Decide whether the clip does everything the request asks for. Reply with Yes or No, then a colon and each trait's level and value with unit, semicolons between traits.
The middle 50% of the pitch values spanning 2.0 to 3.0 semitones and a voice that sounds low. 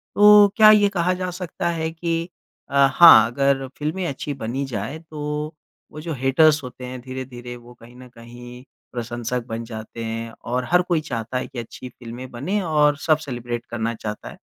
No: average, 4.7 semitones; low, 130 Hz